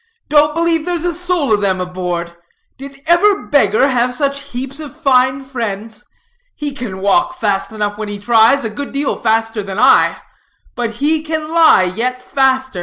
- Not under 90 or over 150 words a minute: No, average, 175 wpm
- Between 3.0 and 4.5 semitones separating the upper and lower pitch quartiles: No, wide, 5.6 semitones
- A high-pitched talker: Yes, very high, 260 Hz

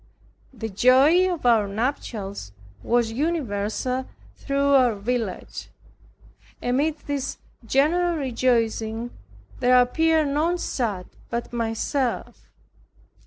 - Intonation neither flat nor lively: Yes, average, 4.2 semitones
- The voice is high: Yes, very high, 250 Hz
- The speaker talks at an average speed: No, slow, 90 wpm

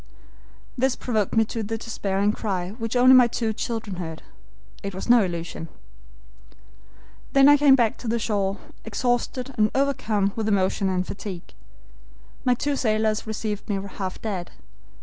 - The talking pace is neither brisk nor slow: Yes, average, 150 wpm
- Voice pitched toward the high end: Yes, high, 215 Hz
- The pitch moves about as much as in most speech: Yes, average, 3.6 semitones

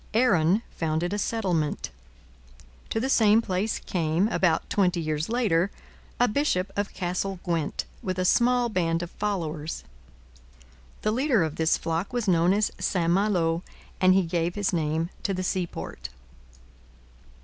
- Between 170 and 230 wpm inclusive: No, average, 145 wpm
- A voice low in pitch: No, medium, 185 Hz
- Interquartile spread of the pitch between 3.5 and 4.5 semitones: Yes, average, 4.0 semitones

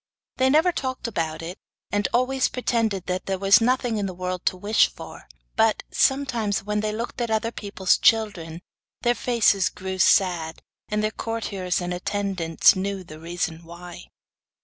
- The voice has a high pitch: Yes, high, 200 Hz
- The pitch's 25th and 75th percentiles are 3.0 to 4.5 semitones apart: Yes, average, 4.0 semitones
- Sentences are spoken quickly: No, average, 165 wpm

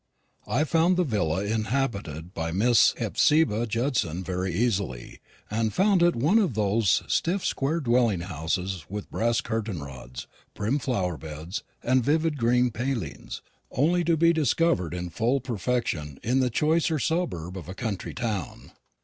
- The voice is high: No, low, 115 Hz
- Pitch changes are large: Yes, wide, 7.1 semitones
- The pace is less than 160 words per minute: Yes, average, 150 wpm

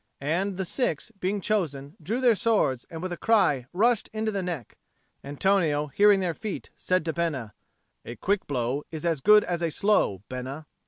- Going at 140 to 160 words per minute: No, average, 180 wpm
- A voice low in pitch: No, medium, 175 Hz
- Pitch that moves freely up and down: Yes, wide, 6.0 semitones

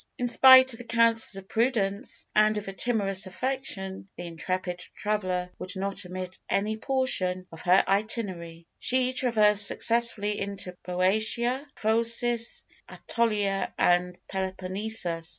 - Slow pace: Yes, slow, 130 wpm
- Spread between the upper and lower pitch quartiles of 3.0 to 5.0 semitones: Yes, average, 3.9 semitones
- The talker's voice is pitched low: No, high, 205 Hz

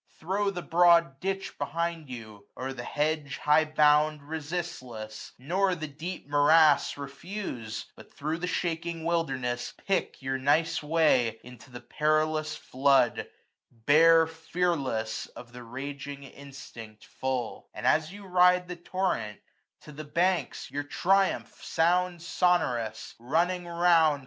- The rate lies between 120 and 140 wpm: Yes, slow, 135 wpm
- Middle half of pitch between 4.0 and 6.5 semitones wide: Yes, average, 4.5 semitones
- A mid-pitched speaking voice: Yes, medium, 155 Hz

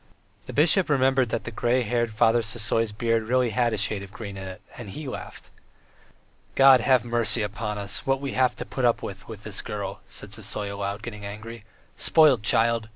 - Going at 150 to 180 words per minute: No, average, 200 wpm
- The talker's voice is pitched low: Yes, low, 115 Hz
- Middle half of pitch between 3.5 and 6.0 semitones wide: No, average, 3.1 semitones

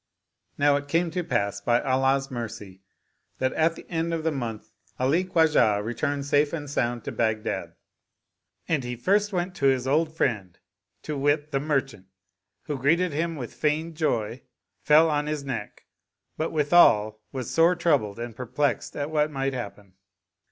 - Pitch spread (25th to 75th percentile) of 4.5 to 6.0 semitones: Yes, average, 4.8 semitones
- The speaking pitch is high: No, medium, 140 Hz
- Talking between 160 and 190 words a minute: Yes, average, 165 wpm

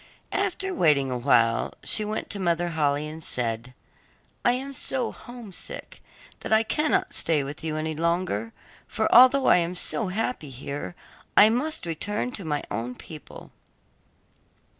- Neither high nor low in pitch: Yes, medium, 170 Hz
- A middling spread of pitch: No, wide, 8.3 semitones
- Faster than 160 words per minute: No, average, 145 wpm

